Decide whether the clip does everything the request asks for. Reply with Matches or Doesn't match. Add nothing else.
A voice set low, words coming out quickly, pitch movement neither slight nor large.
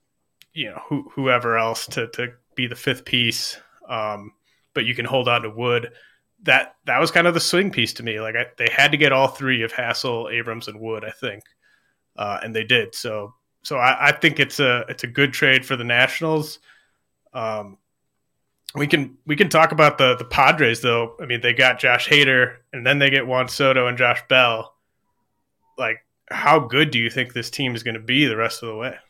Matches